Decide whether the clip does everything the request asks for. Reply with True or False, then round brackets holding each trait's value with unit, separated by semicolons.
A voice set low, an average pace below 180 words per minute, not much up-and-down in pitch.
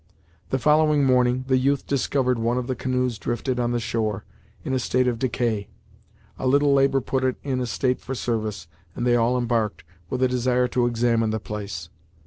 False (125 Hz; 195 wpm; 1.9 semitones)